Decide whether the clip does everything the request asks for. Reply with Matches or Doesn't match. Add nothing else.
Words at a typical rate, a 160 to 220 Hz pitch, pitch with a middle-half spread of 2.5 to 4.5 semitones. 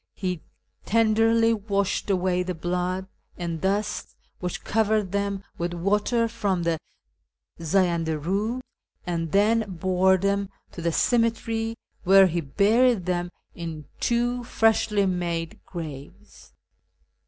Doesn't match